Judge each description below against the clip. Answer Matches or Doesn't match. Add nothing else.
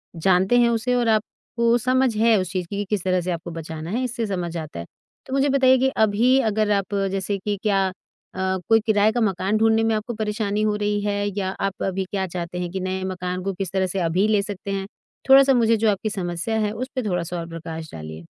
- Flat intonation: Doesn't match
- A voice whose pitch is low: Doesn't match